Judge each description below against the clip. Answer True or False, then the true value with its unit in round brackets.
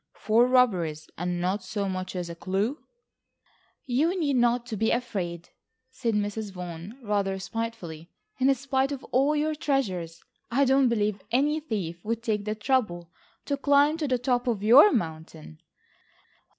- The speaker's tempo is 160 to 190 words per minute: False (150 wpm)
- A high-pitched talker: True (225 Hz)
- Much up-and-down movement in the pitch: True (6.1 semitones)